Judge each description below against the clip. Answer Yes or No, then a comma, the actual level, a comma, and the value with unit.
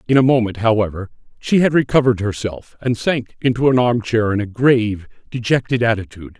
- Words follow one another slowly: No, average, 170 wpm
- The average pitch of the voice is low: Yes, low, 115 Hz